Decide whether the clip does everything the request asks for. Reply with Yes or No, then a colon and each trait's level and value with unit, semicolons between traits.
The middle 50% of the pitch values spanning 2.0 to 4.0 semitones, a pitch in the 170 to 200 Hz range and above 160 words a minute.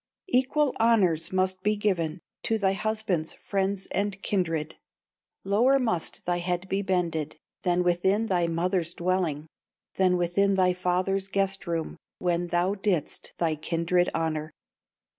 No: narrow, 2.5 semitones; medium, 185 Hz; slow, 135 wpm